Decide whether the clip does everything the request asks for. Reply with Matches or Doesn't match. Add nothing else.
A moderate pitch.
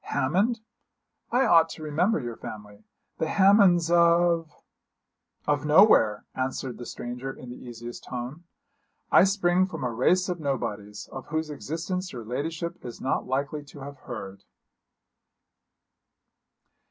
Matches